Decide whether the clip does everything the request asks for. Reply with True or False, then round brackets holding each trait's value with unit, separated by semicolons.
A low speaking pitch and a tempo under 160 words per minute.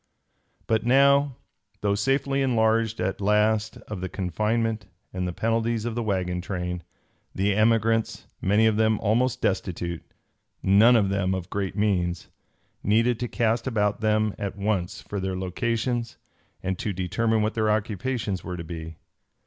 True (105 Hz; 150 wpm)